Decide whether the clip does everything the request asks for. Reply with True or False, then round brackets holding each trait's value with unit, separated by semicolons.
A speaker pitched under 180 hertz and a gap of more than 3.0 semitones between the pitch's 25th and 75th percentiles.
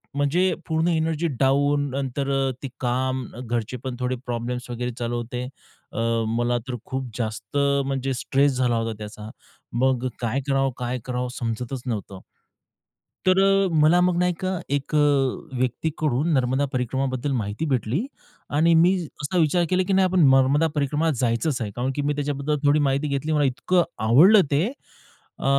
True (135 Hz; 3.5 semitones)